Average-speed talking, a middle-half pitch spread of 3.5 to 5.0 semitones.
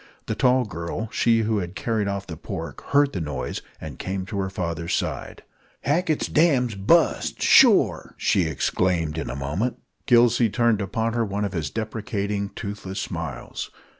Yes: average, 165 wpm; average, 4.6 semitones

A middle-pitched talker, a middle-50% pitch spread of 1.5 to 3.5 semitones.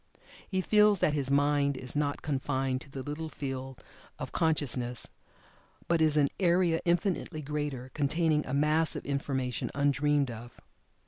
Yes: medium, 145 Hz; average, 2.9 semitones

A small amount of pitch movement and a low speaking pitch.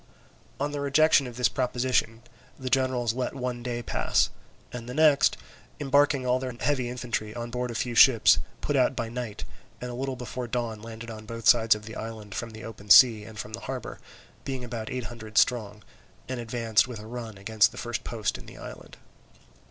Yes: narrow, 2.2 semitones; low, 120 Hz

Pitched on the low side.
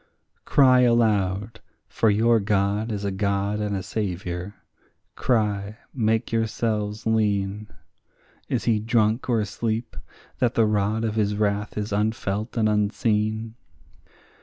Yes: low, 105 Hz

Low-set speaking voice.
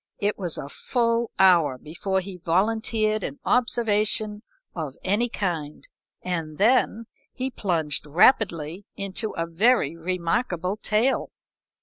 No: high, 190 Hz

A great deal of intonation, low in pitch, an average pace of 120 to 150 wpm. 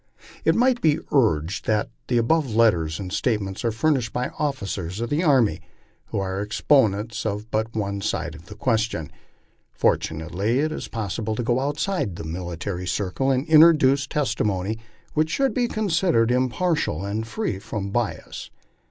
No: wide, 6.2 semitones; low, 115 Hz; average, 160 wpm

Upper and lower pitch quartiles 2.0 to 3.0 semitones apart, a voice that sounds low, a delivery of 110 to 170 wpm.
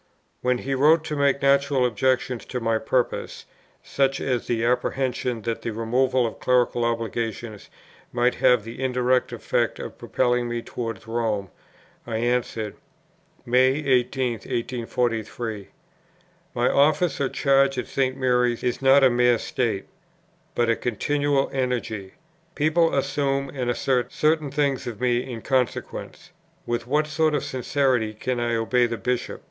Yes: narrow, 2.5 semitones; low, 125 Hz; average, 145 wpm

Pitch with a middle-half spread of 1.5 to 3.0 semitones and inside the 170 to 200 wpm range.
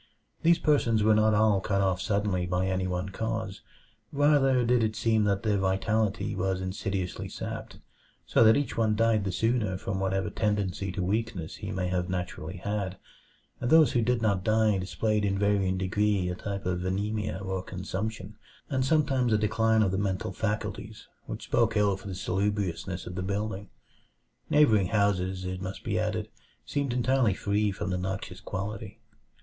Yes: average, 2.7 semitones; average, 175 wpm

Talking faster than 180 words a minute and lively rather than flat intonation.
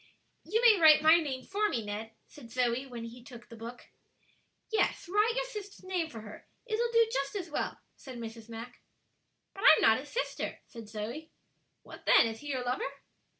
Yes: average, 195 wpm; wide, 9.0 semitones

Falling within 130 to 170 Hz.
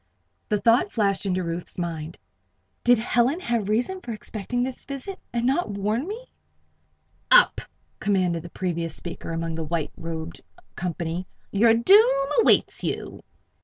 No: high, 210 Hz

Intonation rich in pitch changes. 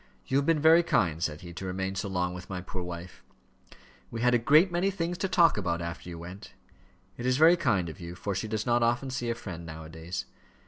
Yes: wide, 7.1 semitones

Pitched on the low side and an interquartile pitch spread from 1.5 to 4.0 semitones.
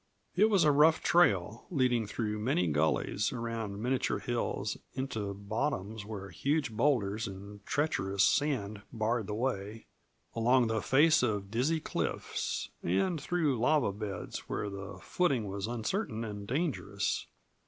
No: low, 115 Hz; wide, 5.4 semitones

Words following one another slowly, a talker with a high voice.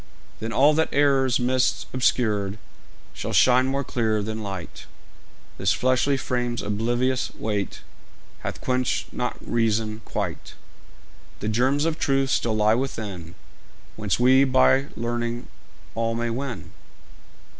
No: slow, 125 wpm; low, 120 Hz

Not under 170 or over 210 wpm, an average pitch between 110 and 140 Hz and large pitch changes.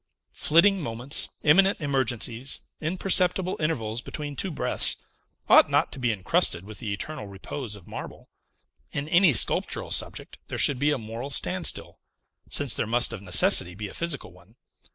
No: average, 155 wpm; low, 135 Hz; wide, 6.3 semitones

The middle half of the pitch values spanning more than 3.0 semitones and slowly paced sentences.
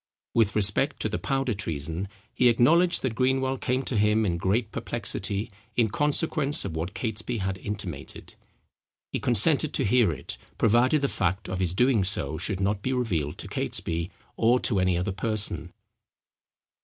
No: average, 4.8 semitones; average, 165 wpm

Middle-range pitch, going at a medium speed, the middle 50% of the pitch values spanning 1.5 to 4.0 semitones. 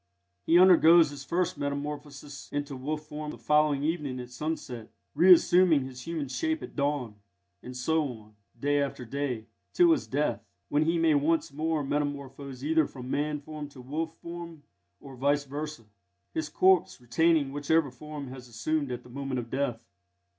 Yes: medium, 145 Hz; average, 170 wpm; average, 3.0 semitones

